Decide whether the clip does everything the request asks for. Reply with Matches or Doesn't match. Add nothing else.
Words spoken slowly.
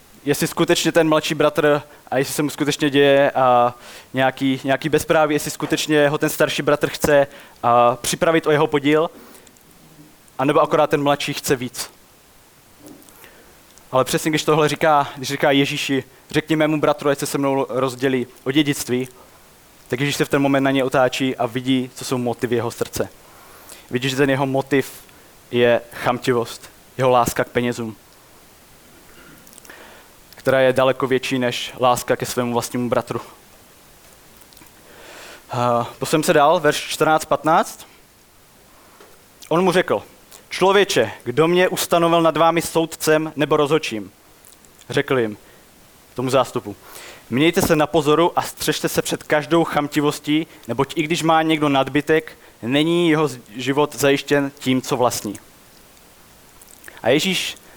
Doesn't match